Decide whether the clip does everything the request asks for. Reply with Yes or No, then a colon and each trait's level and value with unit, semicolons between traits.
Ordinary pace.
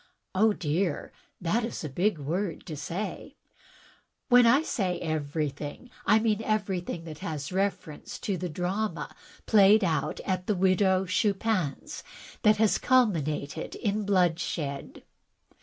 No: slow, 125 wpm